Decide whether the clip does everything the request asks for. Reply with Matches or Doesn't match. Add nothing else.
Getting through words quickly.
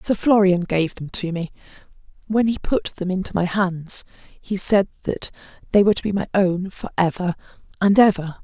Doesn't match